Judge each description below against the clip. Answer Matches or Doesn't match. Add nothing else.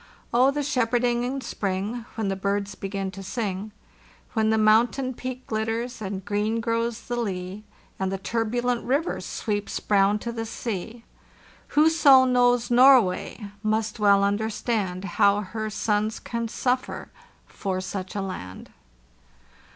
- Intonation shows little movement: Doesn't match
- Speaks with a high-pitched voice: Matches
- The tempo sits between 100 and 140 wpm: Matches